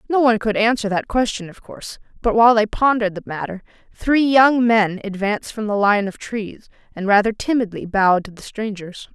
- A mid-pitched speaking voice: No, high, 215 Hz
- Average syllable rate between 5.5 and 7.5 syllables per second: Yes, 5.6 syllables/s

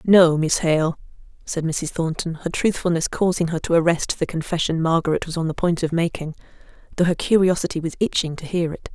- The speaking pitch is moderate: Yes, medium, 165 Hz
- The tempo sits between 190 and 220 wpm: Yes, average, 195 wpm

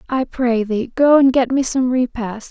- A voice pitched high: Yes, very high, 250 Hz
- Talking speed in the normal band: No, fast, 215 wpm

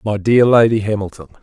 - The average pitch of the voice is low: Yes, low, 105 Hz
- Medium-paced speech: Yes, average, 170 wpm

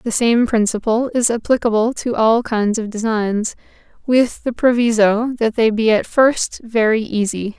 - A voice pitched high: Yes, high, 225 Hz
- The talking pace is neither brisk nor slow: Yes, average, 160 wpm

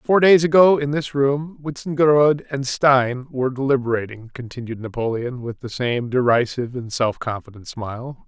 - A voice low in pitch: Yes, low, 130 Hz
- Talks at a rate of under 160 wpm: Yes, average, 150 wpm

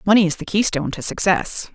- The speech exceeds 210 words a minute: No, fast, 205 wpm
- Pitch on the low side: No, medium, 180 Hz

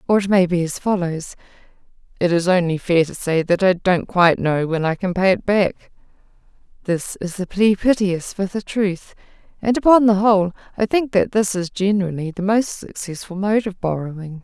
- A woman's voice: Yes, female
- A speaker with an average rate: Yes, average, 195 wpm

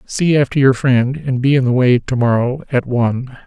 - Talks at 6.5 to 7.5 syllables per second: No, 5.2 syllables/s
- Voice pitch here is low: Yes, low, 130 Hz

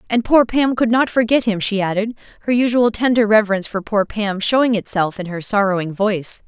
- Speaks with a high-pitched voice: Yes, high, 215 Hz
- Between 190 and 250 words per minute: Yes, fast, 205 wpm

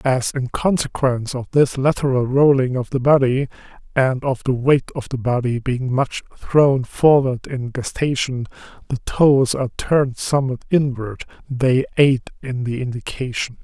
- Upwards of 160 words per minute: No, average, 150 wpm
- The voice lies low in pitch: Yes, low, 130 Hz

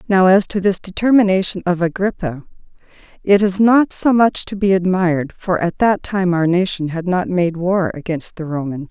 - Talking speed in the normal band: Yes, average, 190 wpm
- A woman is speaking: Yes, female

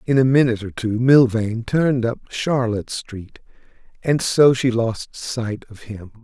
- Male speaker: Yes, male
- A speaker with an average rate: Yes, average, 165 wpm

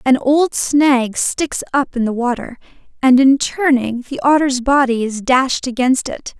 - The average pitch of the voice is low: No, very high, 260 Hz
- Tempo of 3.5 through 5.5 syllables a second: Yes, 4.0 syllables/s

